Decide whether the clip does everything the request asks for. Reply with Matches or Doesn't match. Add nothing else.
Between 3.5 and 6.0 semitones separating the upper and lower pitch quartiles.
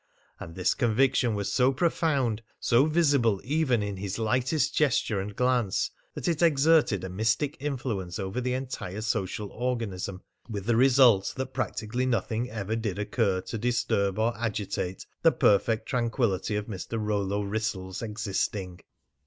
Matches